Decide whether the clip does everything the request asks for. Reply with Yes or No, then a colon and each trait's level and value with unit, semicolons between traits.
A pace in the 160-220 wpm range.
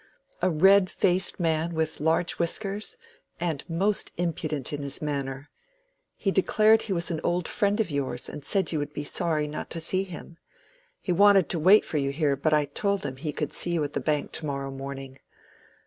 Yes: average, 200 wpm